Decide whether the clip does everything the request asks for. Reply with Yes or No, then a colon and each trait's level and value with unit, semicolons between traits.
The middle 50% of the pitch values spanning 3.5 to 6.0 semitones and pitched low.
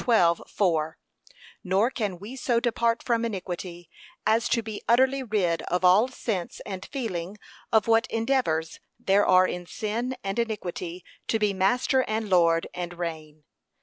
No: average, 4.7 semitones; high, 205 Hz